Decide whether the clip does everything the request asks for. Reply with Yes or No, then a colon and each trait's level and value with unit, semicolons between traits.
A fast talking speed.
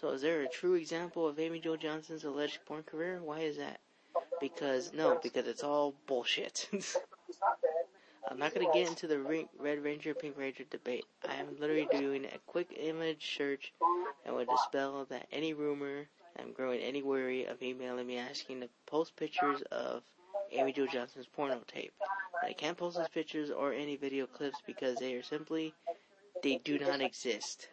No: average, 180 wpm